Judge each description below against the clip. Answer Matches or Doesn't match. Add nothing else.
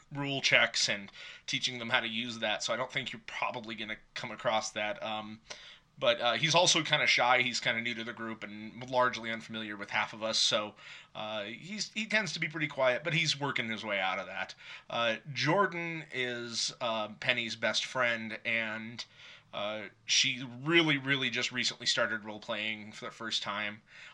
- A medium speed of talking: Matches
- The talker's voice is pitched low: Matches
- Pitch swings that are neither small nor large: Matches